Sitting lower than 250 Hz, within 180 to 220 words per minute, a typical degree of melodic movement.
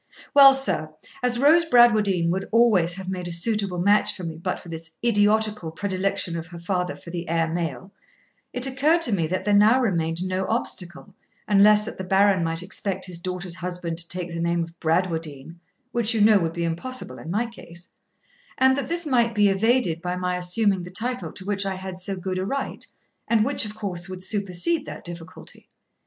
Yes: high, 190 Hz; average, 200 wpm; average, 4.1 semitones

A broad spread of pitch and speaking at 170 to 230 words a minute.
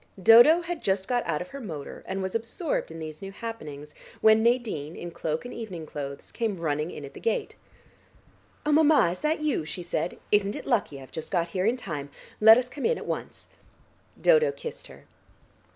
Yes: wide, 7.5 semitones; average, 200 wpm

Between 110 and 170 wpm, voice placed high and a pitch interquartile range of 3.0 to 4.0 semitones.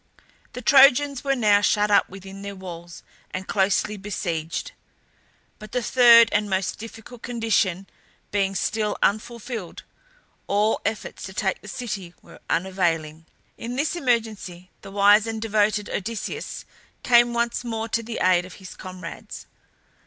Yes: average, 140 wpm; high, 210 Hz; average, 3.5 semitones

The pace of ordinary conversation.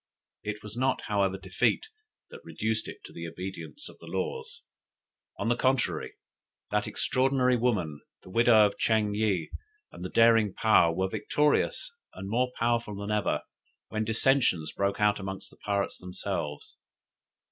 Yes: average, 150 wpm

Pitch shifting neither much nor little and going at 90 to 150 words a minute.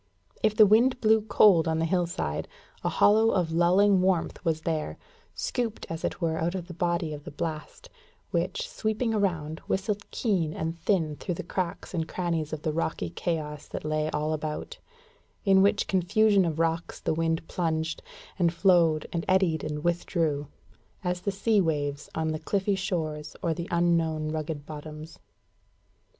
No: average, 3.4 semitones; average, 165 wpm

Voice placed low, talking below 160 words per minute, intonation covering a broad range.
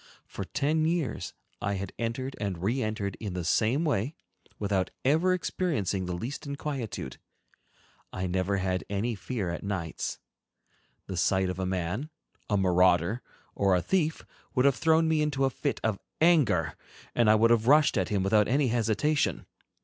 No: low, 110 Hz; average, 165 wpm; wide, 6.8 semitones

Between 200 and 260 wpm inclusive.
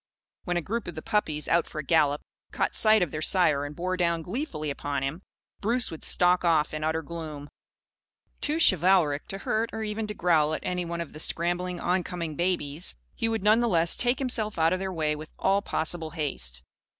Yes: fast, 205 wpm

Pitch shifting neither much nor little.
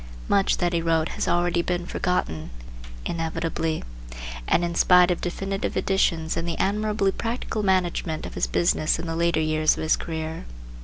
No: narrow, 2.2 semitones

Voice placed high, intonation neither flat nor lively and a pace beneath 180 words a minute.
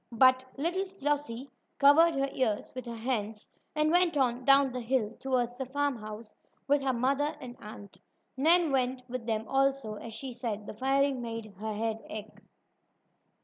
Yes: very high, 255 Hz; average, 3.5 semitones; average, 165 wpm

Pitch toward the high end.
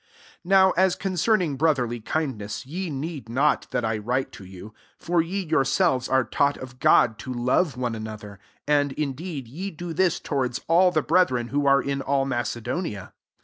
No: medium, 140 Hz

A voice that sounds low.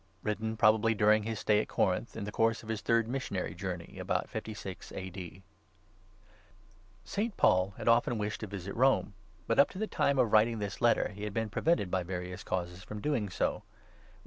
Yes: low, 105 Hz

